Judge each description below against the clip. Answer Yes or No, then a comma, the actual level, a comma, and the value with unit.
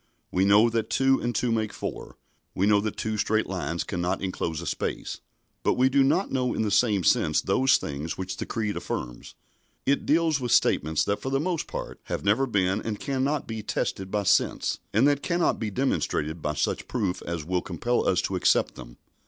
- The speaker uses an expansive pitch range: Yes, wide, 6.1 semitones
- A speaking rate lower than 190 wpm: No, fast, 205 wpm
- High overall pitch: No, low, 105 Hz